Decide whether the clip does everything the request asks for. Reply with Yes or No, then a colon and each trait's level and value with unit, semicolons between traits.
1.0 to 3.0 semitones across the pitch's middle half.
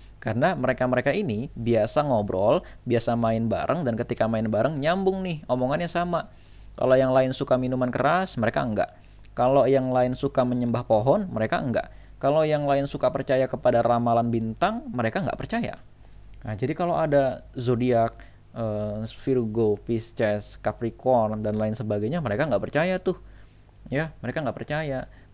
No: average, 3.7 semitones